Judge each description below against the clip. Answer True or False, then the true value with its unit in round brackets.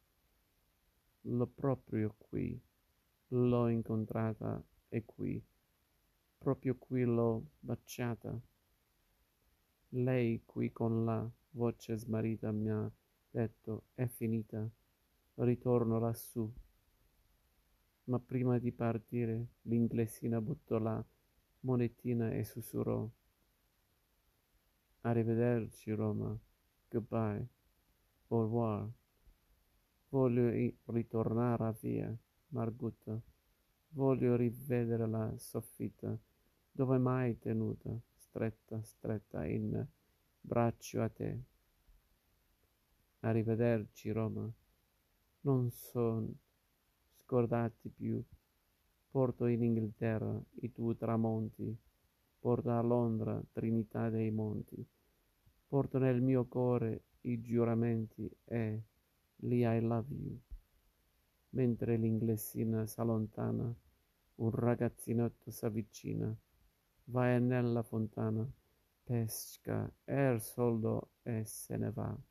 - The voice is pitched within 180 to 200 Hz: False (115 Hz)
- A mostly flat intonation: True (1.8 semitones)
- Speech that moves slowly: True (85 wpm)